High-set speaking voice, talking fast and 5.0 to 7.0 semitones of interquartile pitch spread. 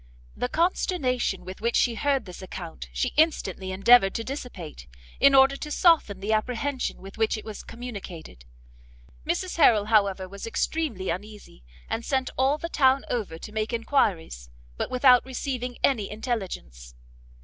No: high, 230 Hz; average, 150 wpm; wide, 5.5 semitones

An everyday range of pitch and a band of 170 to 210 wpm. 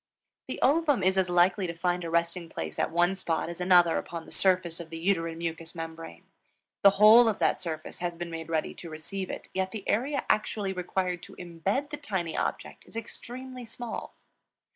Yes: average, 3.2 semitones; average, 195 wpm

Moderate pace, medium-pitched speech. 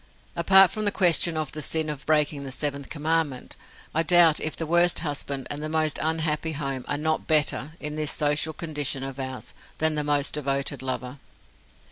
Yes: average, 185 wpm; medium, 150 Hz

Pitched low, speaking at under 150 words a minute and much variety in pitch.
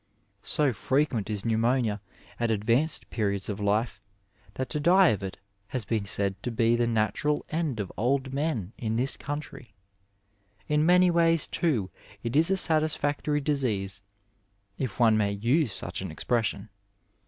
No: low, 120 Hz; average, 155 wpm; wide, 6.0 semitones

